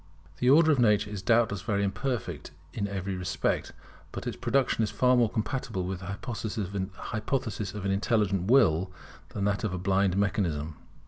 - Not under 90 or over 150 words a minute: No, average, 175 wpm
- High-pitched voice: No, low, 100 Hz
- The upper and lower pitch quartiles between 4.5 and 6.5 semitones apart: No, average, 3.5 semitones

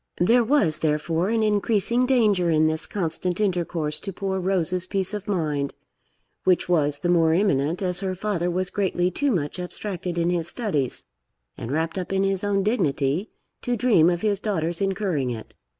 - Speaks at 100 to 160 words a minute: No, average, 175 wpm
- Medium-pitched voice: Yes, medium, 180 Hz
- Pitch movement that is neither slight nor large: Yes, average, 3.9 semitones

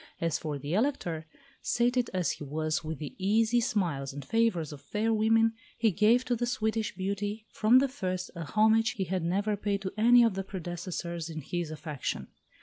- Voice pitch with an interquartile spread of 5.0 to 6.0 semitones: Yes, average, 5.3 semitones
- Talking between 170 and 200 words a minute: Yes, average, 190 wpm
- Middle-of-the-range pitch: No, high, 195 Hz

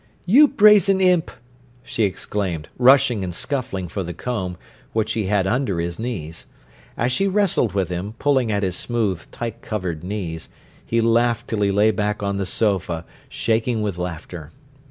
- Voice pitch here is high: No, low, 105 Hz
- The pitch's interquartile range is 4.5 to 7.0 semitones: Yes, average, 4.8 semitones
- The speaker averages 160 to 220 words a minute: Yes, average, 165 wpm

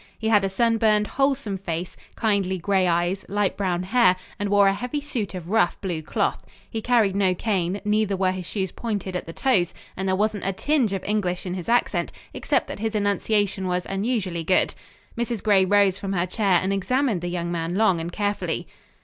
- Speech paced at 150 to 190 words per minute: No, average, 200 wpm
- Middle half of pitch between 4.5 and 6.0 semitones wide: No, average, 2.9 semitones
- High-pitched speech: Yes, high, 195 Hz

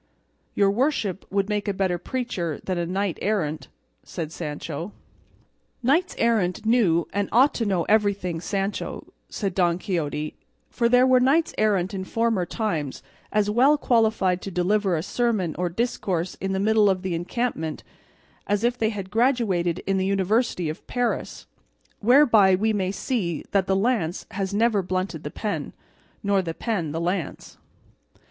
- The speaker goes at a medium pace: Yes, average, 155 wpm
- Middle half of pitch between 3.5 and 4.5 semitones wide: Yes, average, 4.1 semitones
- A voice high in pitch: Yes, high, 195 Hz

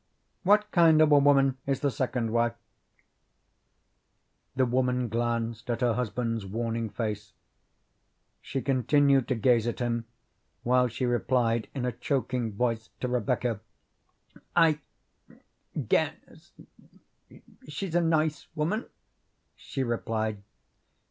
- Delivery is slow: Yes, slow, 115 wpm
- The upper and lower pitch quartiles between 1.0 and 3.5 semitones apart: Yes, average, 3.2 semitones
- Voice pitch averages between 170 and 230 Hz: No, low, 125 Hz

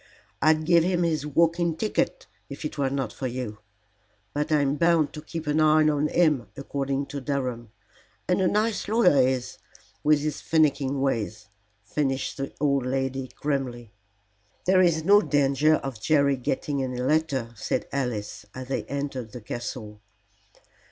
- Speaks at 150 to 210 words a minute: Yes, average, 160 wpm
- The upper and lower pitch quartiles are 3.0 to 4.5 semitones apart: Yes, average, 3.3 semitones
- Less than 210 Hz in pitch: Yes, medium, 140 Hz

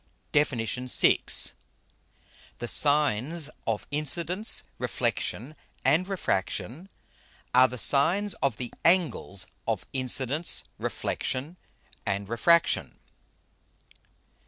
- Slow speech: Yes, slow, 85 wpm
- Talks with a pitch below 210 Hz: Yes, medium, 140 Hz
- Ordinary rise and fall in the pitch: No, wide, 6.0 semitones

